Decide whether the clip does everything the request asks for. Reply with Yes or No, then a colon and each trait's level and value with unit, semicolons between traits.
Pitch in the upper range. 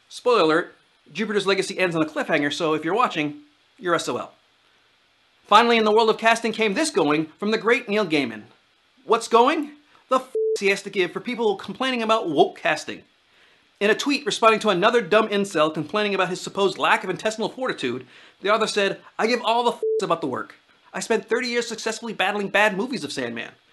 Yes: high, 215 Hz